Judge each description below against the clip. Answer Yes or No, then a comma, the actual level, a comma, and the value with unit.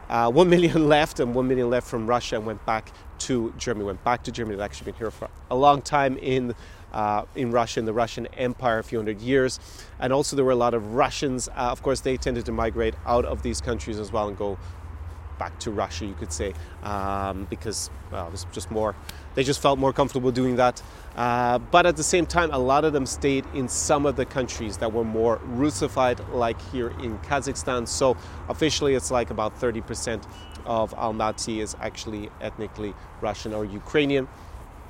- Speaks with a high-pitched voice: No, low, 115 Hz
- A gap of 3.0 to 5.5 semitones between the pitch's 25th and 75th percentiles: Yes, average, 4.2 semitones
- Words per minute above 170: Yes, fast, 205 wpm